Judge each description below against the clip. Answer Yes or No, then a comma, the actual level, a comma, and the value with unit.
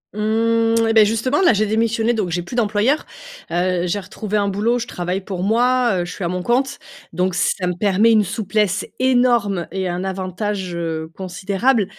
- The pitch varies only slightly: No, average, 3.7 semitones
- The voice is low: No, high, 205 Hz